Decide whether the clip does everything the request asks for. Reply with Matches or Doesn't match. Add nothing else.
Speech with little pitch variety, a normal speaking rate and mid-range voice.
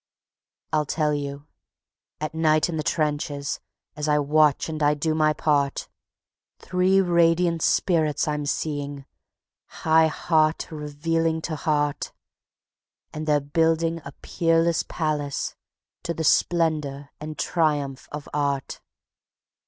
Doesn't match